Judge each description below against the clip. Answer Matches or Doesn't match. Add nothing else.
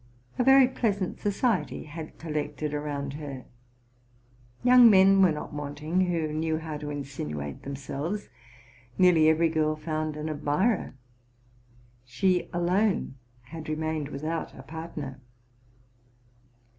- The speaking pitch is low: Doesn't match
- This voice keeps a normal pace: Doesn't match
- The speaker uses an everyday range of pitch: Matches